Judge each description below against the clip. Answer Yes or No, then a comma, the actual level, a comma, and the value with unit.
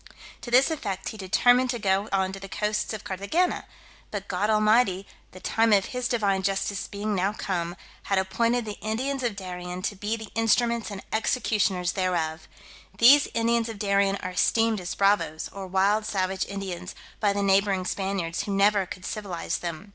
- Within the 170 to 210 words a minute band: Yes, average, 180 wpm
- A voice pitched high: Yes, high, 200 Hz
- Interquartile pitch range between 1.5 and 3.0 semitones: Yes, average, 2.7 semitones